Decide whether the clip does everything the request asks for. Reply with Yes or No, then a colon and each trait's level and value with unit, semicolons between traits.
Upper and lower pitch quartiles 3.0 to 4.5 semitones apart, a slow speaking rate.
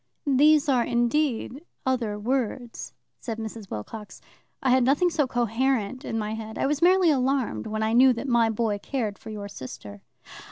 No: average, 3.7 semitones; average, 170 wpm